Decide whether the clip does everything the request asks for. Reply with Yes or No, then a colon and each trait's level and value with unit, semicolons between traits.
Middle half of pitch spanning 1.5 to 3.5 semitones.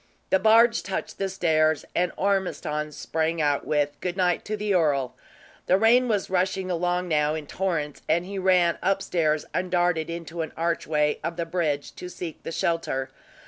Yes: average, 3.2 semitones